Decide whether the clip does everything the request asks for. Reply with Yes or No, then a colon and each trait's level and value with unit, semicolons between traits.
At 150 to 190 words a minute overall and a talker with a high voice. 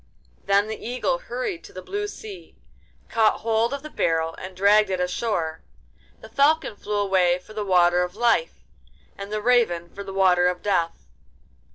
Yes: average, 175 wpm; high, 205 Hz